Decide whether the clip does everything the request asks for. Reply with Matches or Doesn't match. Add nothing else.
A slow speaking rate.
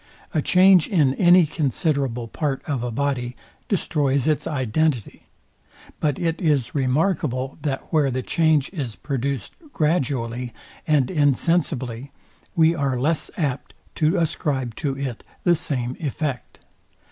Matches